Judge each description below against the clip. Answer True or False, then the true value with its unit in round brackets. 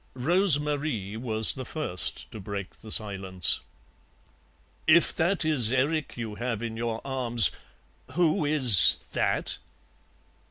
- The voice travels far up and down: True (5.9 semitones)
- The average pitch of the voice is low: True (120 Hz)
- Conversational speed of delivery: False (120 wpm)